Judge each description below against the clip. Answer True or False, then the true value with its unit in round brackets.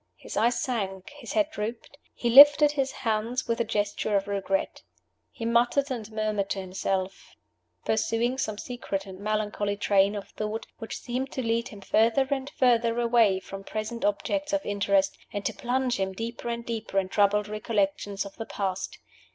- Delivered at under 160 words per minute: False (175 wpm)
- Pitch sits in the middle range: False (220 Hz)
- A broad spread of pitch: False (3.1 semitones)